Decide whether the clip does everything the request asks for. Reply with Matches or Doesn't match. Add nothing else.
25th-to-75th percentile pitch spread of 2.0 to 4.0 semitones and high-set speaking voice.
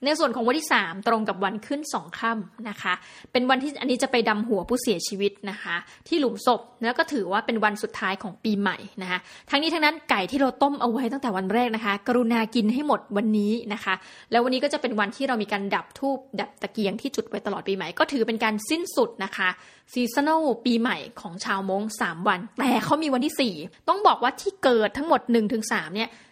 Doesn't match